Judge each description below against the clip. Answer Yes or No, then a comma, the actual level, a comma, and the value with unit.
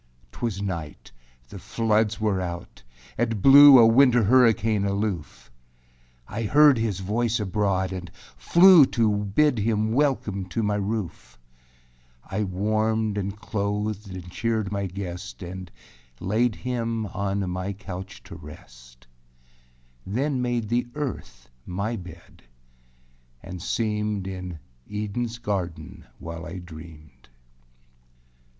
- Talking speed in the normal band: No, slow, 120 wpm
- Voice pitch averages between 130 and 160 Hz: No, low, 105 Hz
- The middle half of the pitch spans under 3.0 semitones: No, average, 3.6 semitones